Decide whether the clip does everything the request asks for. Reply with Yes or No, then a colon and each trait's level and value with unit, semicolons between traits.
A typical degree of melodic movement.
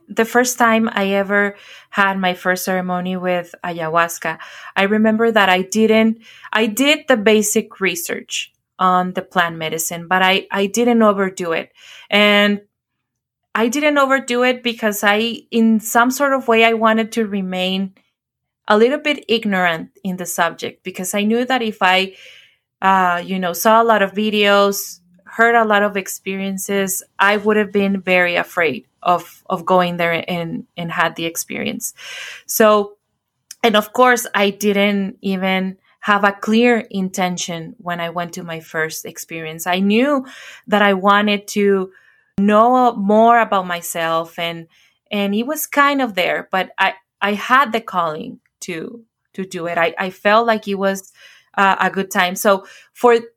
Yes: average, 3.5 semitones